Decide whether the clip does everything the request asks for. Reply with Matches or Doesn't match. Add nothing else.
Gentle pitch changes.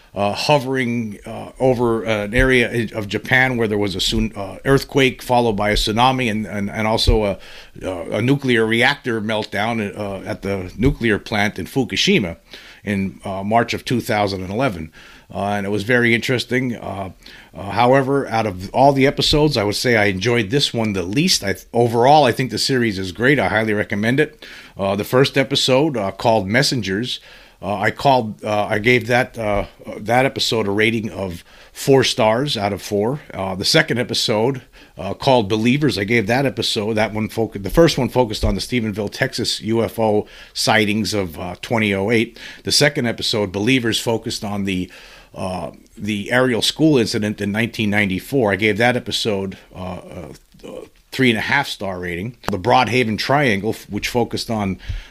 Doesn't match